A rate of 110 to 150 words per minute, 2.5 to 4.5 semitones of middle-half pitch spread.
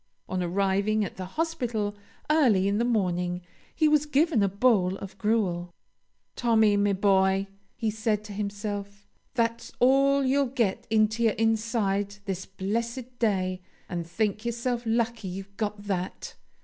Yes: average, 145 wpm; average, 3.3 semitones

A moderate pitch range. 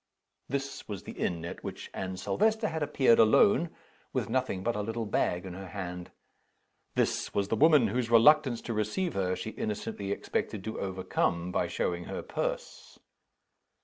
No: wide, 6.3 semitones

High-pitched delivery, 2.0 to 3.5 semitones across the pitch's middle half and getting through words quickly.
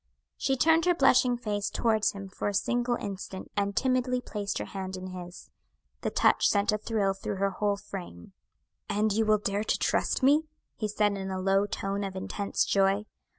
No: high, 205 Hz; average, 2.8 semitones; average, 190 wpm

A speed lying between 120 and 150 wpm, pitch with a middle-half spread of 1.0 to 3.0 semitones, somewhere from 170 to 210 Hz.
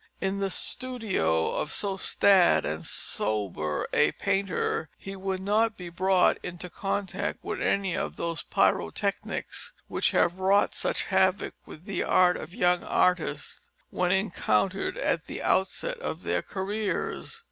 Yes: average, 140 wpm; narrow, 2.6 semitones; high, 190 Hz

